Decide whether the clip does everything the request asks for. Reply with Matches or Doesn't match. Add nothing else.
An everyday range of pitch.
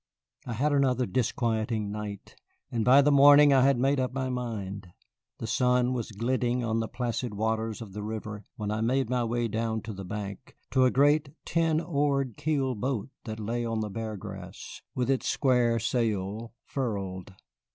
Matches